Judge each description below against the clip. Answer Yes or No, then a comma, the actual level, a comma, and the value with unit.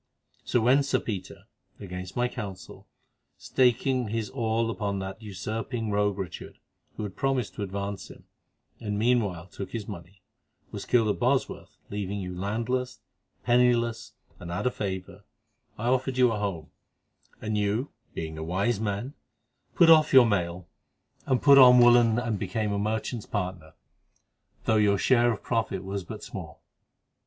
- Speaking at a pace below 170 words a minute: Yes, average, 150 wpm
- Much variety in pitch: No, average, 3.8 semitones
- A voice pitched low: Yes, low, 110 Hz